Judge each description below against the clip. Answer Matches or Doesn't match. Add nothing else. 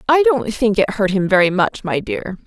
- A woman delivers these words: Matches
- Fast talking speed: Matches